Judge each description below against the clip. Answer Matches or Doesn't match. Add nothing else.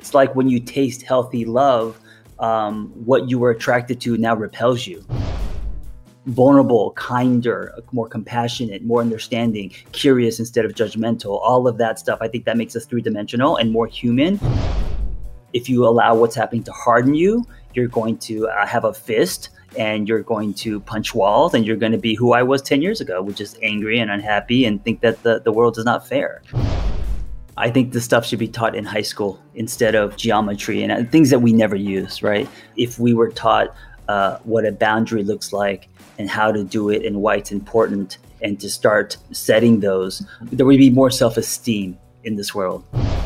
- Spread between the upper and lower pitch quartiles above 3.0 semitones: Doesn't match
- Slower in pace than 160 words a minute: Doesn't match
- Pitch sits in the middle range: Doesn't match